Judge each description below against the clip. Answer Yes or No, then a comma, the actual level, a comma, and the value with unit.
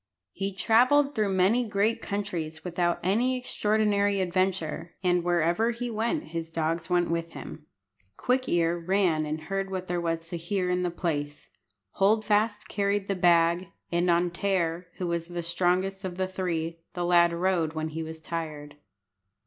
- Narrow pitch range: No, average, 3.0 semitones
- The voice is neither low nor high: Yes, medium, 180 Hz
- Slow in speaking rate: No, average, 165 wpm